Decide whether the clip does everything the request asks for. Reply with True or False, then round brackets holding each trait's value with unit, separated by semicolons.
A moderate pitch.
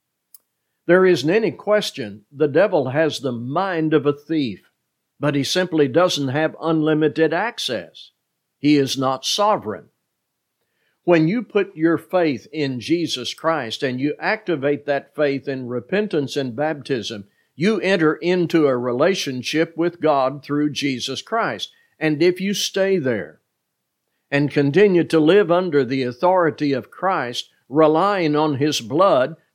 True (155 Hz)